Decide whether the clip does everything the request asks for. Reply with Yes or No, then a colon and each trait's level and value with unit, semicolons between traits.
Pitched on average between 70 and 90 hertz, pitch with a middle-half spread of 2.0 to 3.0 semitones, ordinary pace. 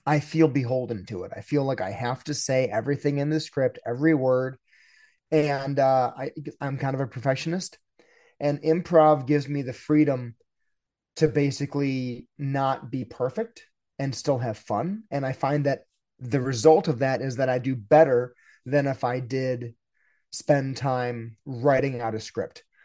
No: low, 135 Hz; average, 2.7 semitones; average, 170 wpm